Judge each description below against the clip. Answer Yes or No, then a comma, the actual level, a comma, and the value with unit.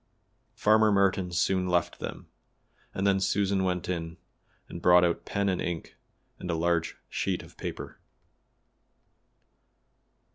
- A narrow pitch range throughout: Yes, narrow, 2.0 semitones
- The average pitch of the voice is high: No, very low, 90 Hz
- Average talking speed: No, slow, 130 wpm